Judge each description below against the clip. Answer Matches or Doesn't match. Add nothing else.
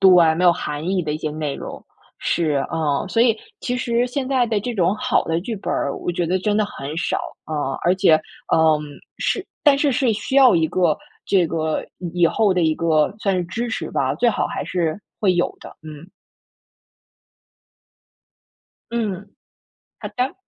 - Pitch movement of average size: Doesn't match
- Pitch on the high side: Doesn't match